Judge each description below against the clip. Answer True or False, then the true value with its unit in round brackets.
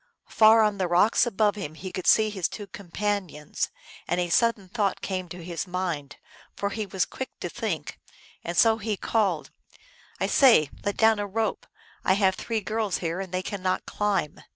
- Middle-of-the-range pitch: False (195 Hz)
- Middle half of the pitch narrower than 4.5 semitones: True (3.2 semitones)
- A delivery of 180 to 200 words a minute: True (185 wpm)